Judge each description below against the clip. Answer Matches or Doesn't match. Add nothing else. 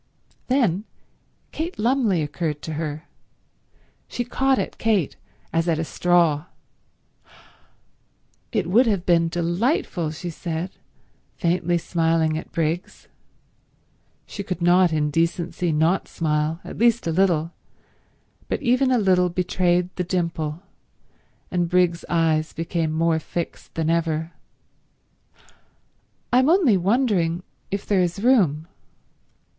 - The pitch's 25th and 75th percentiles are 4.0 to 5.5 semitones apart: Doesn't match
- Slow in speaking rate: Matches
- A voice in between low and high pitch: Matches